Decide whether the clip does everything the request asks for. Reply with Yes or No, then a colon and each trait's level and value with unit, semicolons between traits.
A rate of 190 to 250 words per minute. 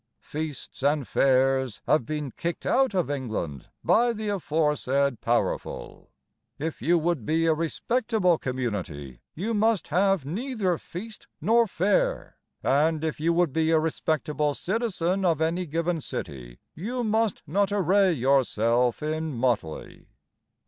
No: slow, 135 wpm